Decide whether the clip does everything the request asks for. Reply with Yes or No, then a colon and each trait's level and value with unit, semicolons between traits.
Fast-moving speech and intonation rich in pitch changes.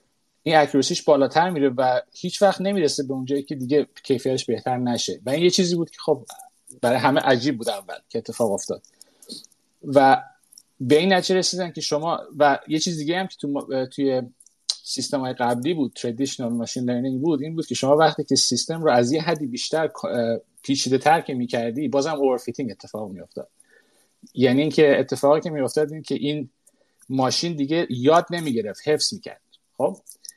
No: fast, 175 wpm; average, 3.9 semitones